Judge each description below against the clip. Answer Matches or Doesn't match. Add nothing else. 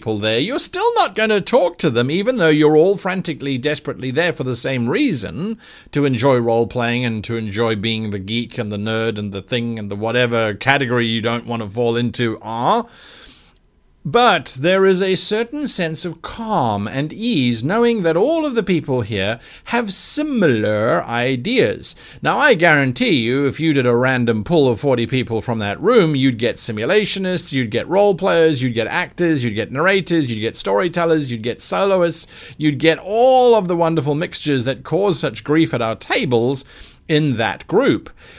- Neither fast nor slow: Matches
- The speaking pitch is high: Doesn't match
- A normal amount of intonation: Doesn't match